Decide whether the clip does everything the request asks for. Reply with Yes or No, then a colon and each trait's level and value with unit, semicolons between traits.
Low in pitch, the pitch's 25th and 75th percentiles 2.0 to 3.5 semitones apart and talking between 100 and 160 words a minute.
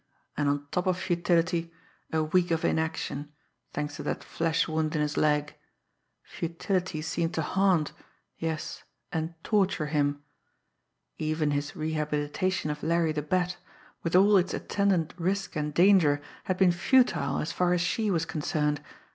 No: medium, 165 Hz; average, 3.1 semitones; average, 150 wpm